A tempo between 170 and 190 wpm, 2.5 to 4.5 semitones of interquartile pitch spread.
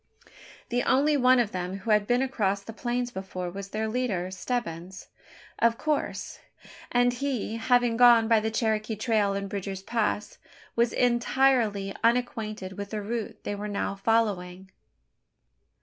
No: average, 150 wpm; average, 3.5 semitones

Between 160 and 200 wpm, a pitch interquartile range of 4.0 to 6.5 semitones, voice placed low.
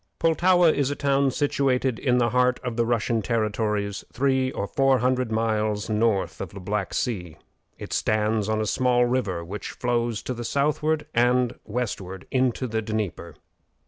No: average, 165 wpm; average, 3.3 semitones; low, 120 Hz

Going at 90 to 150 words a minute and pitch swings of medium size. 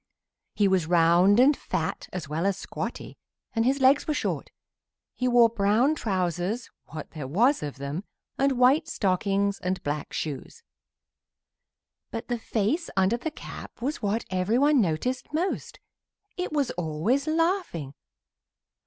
No: average, 140 wpm; wide, 7.1 semitones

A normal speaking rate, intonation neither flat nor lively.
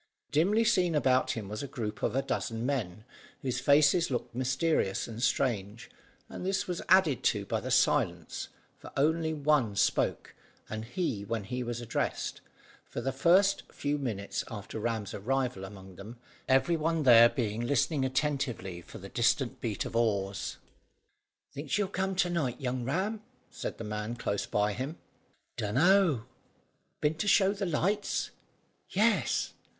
No: average, 155 wpm; wide, 6.5 semitones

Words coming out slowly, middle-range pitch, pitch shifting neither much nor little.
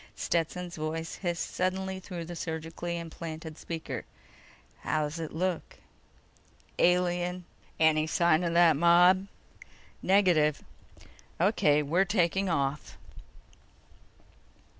No: slow, 95 wpm; medium, 170 Hz; narrow, 2.2 semitones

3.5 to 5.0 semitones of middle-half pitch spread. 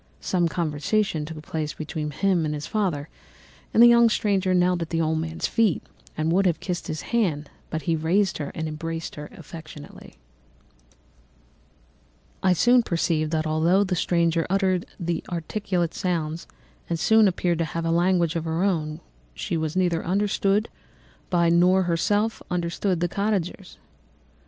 No: average, 3.0 semitones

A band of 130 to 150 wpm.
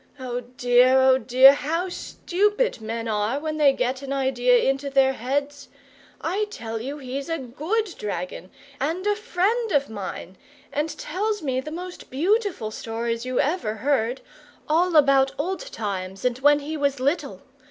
No: average, 160 wpm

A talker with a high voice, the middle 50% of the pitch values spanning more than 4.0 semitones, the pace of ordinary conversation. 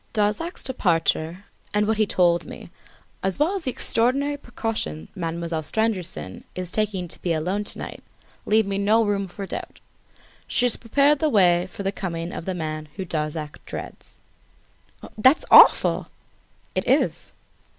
Yes: high, 195 Hz; average, 4.8 semitones; average, 155 wpm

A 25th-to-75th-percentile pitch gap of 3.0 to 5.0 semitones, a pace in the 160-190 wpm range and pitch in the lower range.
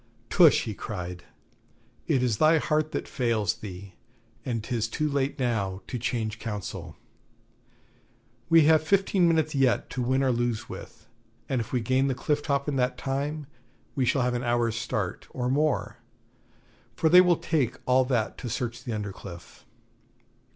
Yes: average, 4.4 semitones; average, 165 wpm; low, 125 Hz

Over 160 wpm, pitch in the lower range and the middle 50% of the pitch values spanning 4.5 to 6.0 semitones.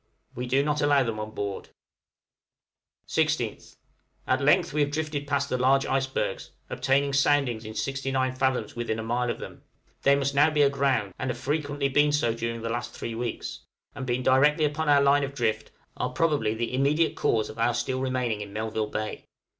No: average, 190 wpm; low, 130 Hz; average, 3.3 semitones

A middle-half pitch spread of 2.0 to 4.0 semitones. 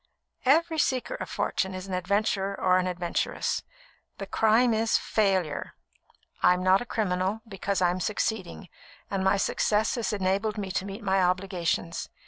Yes: average, 2.8 semitones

